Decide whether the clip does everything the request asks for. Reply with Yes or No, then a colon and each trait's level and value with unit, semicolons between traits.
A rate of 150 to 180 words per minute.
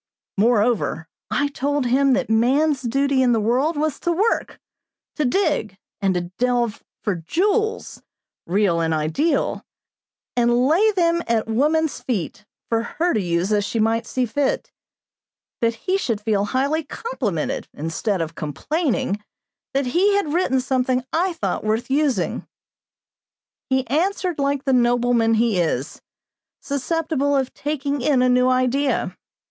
No: average, 140 wpm